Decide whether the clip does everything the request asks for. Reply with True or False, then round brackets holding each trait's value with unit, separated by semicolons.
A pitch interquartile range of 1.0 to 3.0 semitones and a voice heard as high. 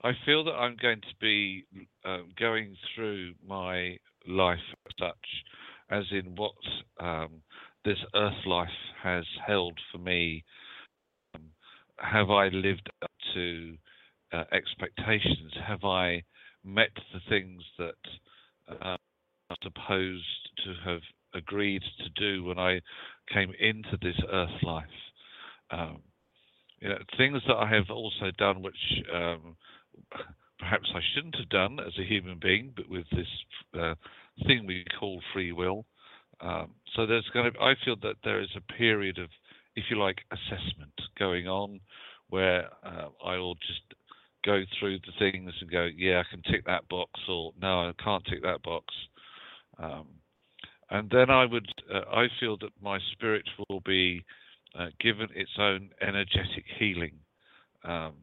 False (2.7 semitones; 95 Hz)